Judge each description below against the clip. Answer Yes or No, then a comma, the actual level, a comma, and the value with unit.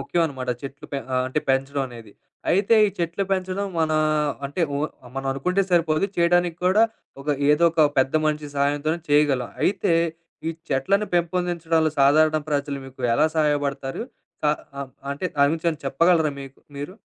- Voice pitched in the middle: Yes, medium, 155 Hz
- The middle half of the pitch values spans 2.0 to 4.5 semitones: Yes, average, 3.6 semitones